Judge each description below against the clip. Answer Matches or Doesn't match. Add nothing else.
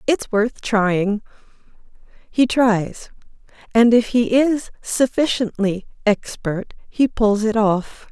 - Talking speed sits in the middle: Doesn't match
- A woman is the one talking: Matches